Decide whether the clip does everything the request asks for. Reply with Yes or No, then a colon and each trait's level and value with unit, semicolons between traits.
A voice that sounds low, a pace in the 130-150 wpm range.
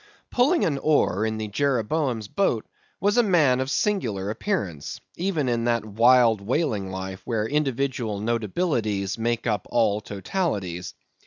Yes: low, 115 Hz; average, 145 wpm